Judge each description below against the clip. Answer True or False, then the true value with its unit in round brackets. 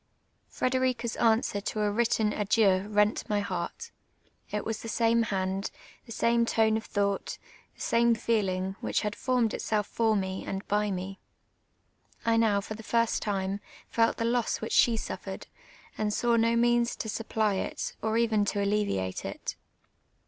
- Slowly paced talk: False (170 wpm)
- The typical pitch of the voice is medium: False (215 Hz)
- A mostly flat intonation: True (2.3 semitones)